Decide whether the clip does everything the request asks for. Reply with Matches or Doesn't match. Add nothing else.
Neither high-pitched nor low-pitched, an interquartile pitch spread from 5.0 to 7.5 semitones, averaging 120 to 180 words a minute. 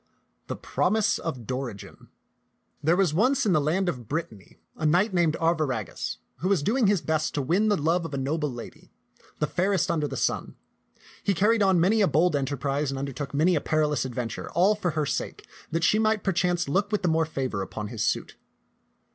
Doesn't match